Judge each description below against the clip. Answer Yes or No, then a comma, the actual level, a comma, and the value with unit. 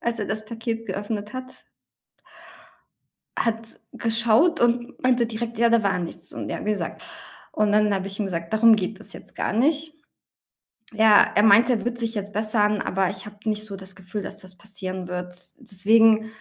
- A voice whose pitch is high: Yes, high, 215 Hz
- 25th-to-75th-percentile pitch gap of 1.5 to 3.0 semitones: Yes, narrow, 2.5 semitones